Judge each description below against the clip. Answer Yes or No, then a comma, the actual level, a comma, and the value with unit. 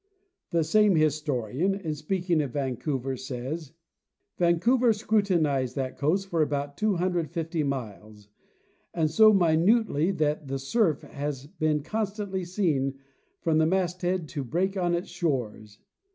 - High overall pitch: No, medium, 160 Hz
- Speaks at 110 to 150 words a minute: Yes, average, 140 wpm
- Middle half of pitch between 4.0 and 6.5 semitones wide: Yes, average, 4.9 semitones